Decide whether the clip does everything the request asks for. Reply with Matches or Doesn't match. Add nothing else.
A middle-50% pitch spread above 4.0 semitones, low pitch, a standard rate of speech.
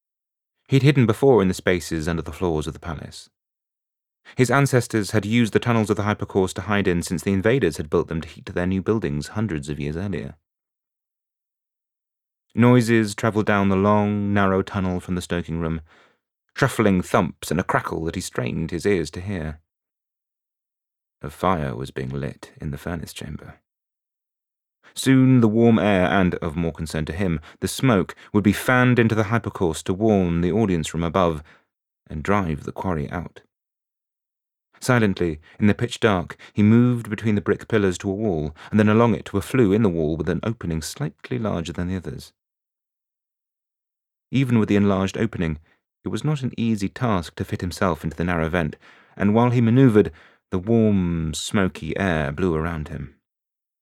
Matches